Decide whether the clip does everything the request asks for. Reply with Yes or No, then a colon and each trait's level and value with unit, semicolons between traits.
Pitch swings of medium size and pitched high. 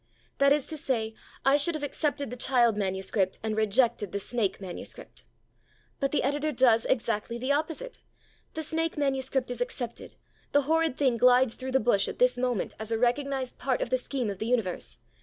Yes: average, 3.8 semitones; very high, 250 Hz